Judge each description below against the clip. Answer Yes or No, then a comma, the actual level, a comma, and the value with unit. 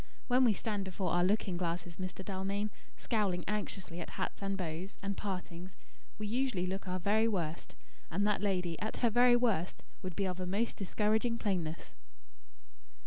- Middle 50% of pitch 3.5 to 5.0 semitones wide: No, average, 2.8 semitones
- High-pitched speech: Yes, high, 195 Hz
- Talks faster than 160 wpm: Yes, average, 170 wpm